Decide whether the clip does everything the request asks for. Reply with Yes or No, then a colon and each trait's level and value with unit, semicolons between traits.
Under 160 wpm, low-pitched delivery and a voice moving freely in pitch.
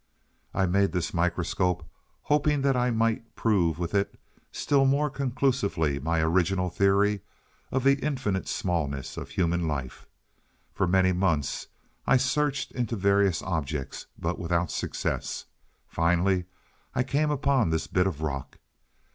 Yes: slow, 135 wpm; very low, 95 Hz; wide, 6.9 semitones